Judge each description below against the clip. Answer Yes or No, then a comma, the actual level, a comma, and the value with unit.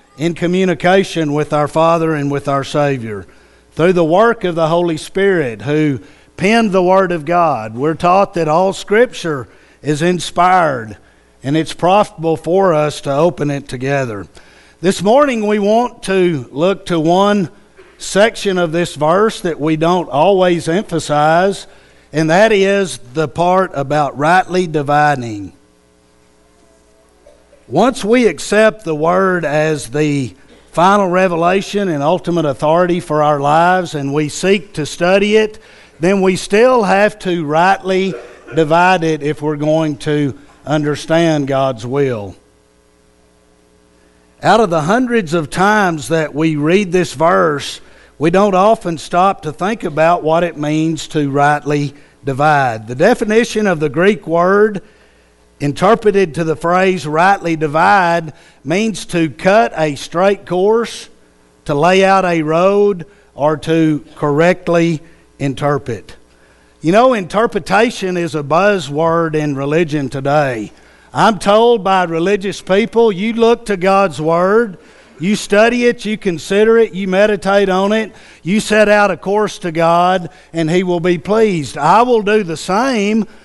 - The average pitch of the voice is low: No, medium, 170 Hz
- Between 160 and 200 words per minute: No, average, 140 wpm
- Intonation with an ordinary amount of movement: Yes, average, 4.8 semitones